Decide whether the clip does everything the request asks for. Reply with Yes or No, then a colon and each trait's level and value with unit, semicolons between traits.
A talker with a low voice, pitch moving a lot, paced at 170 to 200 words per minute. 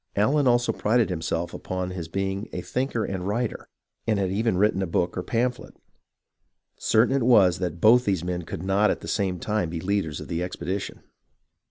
No: very low, 95 Hz; average, 3.9 semitones; average, 190 wpm